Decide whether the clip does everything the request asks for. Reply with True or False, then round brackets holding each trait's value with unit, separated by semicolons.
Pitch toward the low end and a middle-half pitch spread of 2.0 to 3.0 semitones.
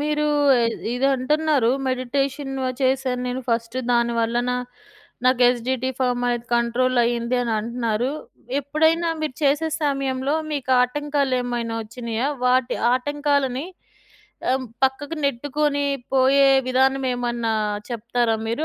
False (255 Hz; 2.6 semitones)